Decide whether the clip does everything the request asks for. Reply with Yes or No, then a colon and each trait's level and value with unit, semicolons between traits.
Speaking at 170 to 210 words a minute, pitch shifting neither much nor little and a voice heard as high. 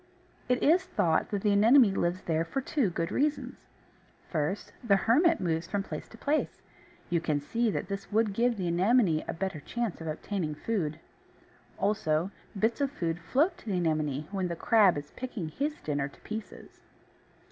No: average, 180 wpm; wide, 6.2 semitones; high, 195 Hz